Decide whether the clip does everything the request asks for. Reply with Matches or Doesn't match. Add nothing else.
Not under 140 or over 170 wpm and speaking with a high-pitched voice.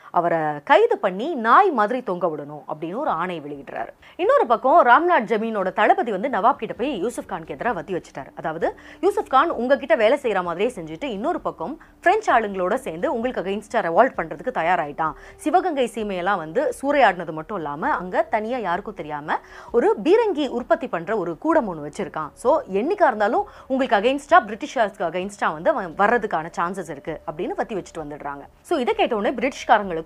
Matches